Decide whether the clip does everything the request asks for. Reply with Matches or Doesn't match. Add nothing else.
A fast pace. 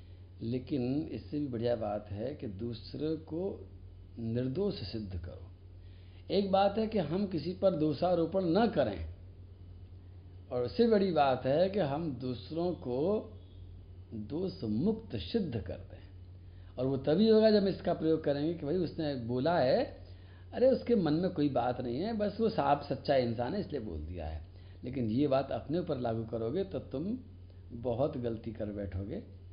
Doesn't match